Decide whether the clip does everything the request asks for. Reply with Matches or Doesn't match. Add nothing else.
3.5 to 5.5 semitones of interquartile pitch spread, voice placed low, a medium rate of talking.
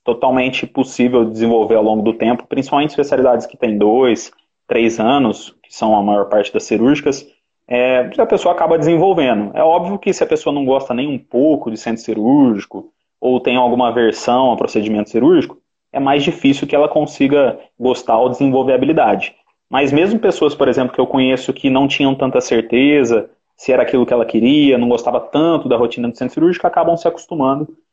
Doesn't match